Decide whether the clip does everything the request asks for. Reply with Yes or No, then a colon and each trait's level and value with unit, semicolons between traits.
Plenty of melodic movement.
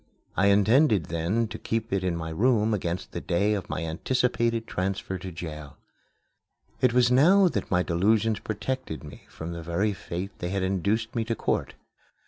No: average, 4.8 semitones